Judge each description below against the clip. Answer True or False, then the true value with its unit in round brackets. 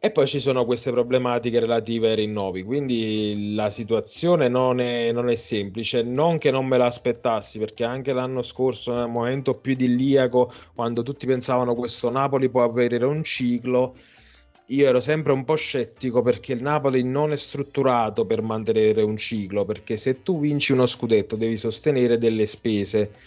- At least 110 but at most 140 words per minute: False (170 wpm)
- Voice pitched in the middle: False (125 Hz)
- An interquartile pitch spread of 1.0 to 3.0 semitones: True (2.5 semitones)